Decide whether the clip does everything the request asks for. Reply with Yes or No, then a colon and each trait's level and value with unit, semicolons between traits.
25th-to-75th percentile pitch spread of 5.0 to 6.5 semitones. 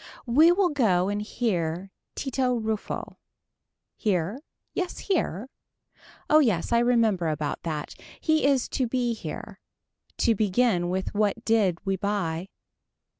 Yes: average, 5.3 semitones